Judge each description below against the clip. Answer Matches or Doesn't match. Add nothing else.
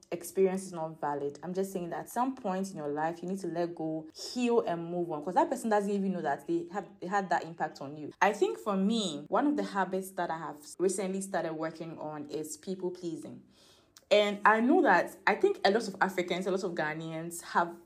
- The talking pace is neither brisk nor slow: Doesn't match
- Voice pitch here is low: Doesn't match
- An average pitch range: Matches